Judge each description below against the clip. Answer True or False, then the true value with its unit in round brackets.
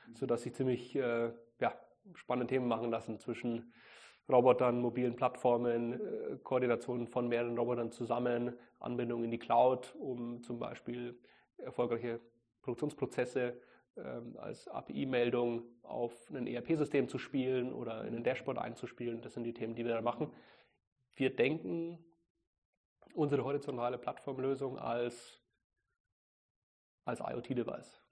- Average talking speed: False (120 wpm)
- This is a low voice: True (120 Hz)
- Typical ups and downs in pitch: False (1.2 semitones)